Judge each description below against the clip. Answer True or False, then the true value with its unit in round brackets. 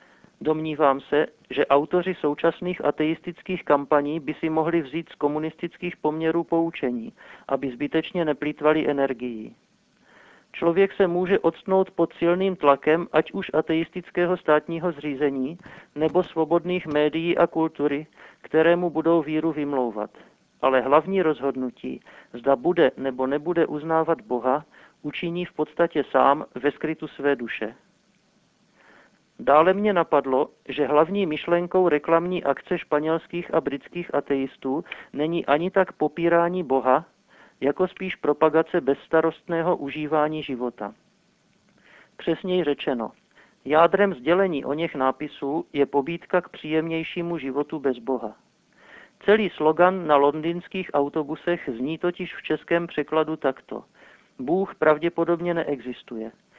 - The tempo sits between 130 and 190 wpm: False (115 wpm)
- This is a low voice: False (160 Hz)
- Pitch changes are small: False (3.0 semitones)